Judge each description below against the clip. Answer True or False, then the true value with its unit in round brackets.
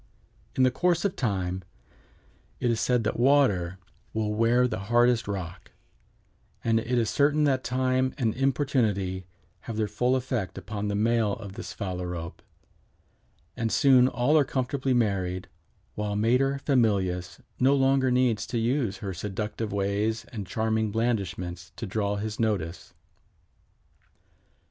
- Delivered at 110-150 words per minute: True (140 wpm)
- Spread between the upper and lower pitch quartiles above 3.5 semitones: True (4.2 semitones)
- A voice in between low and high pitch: False (110 Hz)